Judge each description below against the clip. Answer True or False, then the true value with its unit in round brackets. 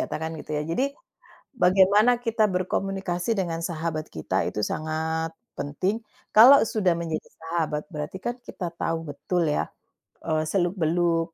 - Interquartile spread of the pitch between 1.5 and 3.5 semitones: True (3.1 semitones)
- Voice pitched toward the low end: False (170 Hz)